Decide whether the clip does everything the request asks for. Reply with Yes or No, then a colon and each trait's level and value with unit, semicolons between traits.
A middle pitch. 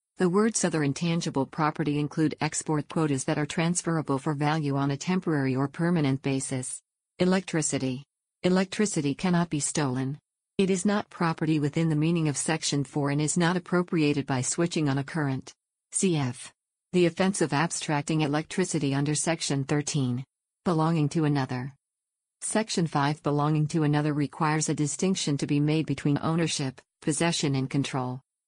Yes: medium, 150 Hz